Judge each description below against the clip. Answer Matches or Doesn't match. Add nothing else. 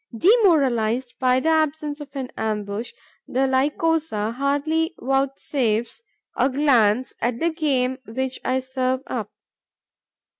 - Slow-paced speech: Matches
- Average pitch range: Matches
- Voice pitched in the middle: Doesn't match